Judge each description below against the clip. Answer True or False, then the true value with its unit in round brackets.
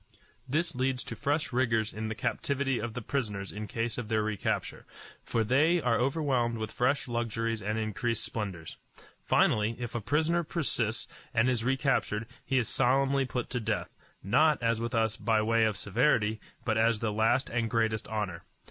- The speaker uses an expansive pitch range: False (3.1 semitones)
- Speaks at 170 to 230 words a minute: True (175 wpm)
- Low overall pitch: True (115 Hz)